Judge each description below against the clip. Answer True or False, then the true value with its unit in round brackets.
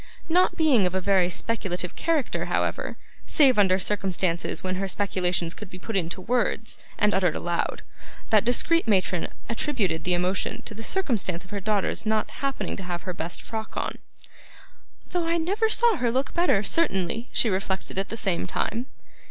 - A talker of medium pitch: False (205 Hz)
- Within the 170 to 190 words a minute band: True (175 wpm)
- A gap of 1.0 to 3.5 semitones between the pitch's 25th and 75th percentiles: False (5.3 semitones)